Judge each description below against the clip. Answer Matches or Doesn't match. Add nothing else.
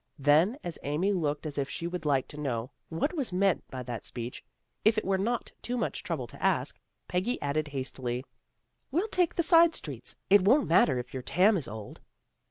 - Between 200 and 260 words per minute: Matches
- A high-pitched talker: Doesn't match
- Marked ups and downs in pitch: Matches